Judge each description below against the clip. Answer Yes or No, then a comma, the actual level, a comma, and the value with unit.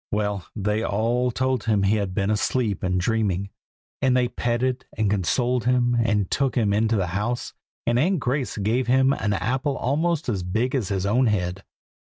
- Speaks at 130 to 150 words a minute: No, average, 185 wpm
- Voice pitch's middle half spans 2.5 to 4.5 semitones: Yes, average, 3.9 semitones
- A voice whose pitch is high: No, low, 115 Hz